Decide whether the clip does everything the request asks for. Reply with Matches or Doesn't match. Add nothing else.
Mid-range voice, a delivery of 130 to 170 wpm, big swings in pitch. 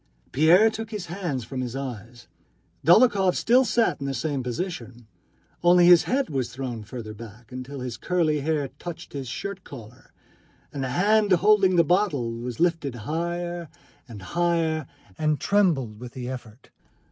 Matches